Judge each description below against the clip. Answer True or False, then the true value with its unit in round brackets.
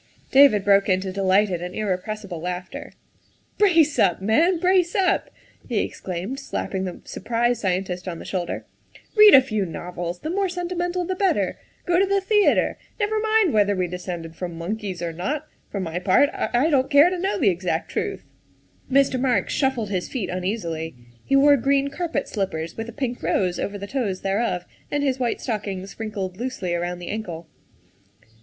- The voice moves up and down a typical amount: False (7.7 semitones)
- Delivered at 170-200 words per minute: True (185 wpm)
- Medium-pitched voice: False (215 Hz)